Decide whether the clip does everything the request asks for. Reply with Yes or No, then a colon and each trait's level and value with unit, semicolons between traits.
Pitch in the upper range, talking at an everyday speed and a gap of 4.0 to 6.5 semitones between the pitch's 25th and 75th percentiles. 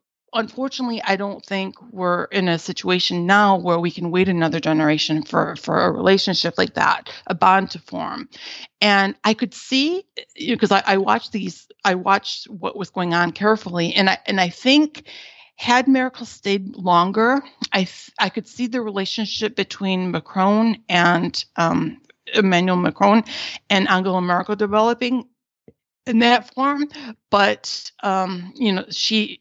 Yes: high, 200 Hz; average, 155 wpm; average, 4.4 semitones